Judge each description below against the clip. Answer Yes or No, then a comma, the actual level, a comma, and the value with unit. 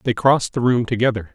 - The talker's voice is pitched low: Yes, low, 120 Hz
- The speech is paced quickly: Yes, fast, 225 wpm